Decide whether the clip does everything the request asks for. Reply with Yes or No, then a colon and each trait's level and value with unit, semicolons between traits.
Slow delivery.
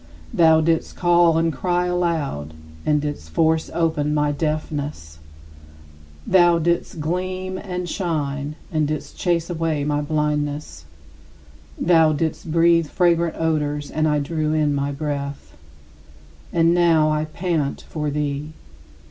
Yes: slow, 125 wpm